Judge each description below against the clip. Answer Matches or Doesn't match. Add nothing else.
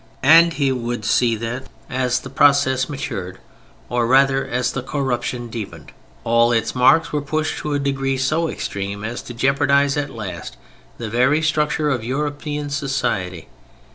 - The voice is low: Matches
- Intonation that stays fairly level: Doesn't match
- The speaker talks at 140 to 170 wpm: Matches